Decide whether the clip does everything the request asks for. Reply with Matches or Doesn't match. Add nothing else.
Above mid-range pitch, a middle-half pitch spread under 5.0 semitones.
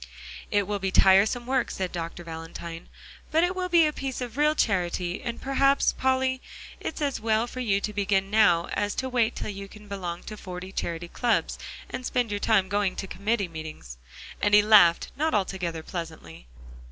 Doesn't match